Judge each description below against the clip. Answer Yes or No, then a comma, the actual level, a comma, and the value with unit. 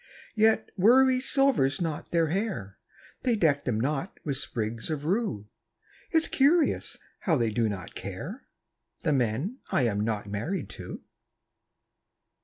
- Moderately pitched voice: Yes, medium, 155 Hz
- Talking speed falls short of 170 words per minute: Yes, slow, 135 wpm